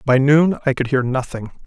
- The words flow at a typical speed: No, fast, 215 wpm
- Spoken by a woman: No, male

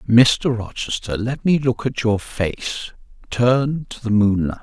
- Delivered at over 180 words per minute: No, average, 155 wpm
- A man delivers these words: Yes, male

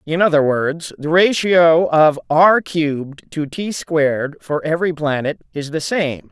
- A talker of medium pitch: Yes, medium, 160 Hz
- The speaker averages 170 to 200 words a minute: No, average, 160 wpm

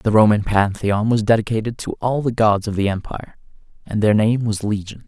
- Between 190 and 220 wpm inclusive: Yes, average, 200 wpm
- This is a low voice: Yes, low, 110 Hz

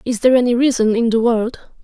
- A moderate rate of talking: No, fast, 230 wpm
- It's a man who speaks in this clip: No, female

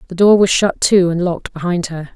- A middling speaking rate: No, fast, 250 wpm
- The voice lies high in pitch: No, medium, 180 Hz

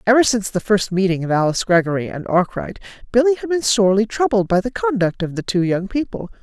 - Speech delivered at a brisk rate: Yes, fast, 215 wpm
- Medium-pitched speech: No, high, 205 Hz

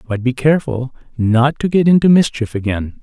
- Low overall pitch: Yes, low, 130 Hz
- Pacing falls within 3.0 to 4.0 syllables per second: No, 5.4 syllables/s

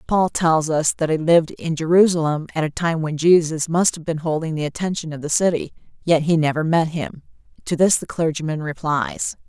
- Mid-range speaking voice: Yes, medium, 160 Hz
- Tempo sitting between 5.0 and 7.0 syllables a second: Yes, 5.3 syllables/s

